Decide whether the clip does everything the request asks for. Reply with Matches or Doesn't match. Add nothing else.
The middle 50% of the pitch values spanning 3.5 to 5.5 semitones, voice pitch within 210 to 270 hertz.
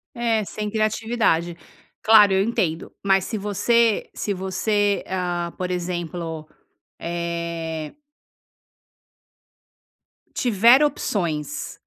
Doesn't match